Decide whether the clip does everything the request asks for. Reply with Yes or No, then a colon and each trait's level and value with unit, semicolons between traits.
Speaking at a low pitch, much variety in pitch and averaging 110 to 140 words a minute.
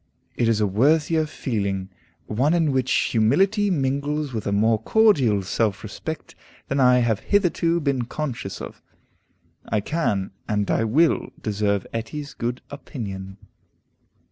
Yes: low, 125 Hz; wide, 6.3 semitones; slow, 135 wpm